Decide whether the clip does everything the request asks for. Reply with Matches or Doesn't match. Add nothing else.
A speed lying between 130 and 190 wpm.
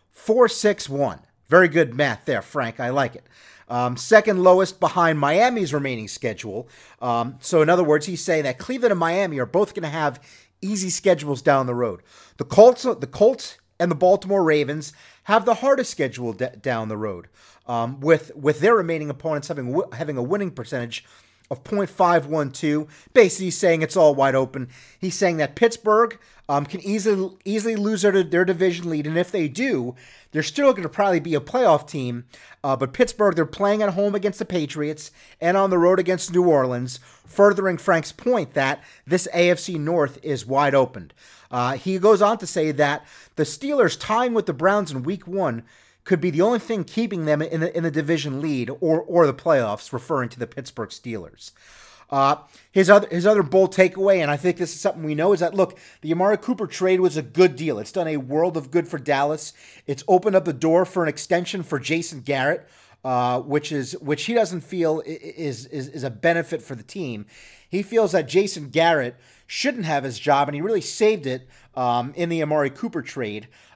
Doesn't match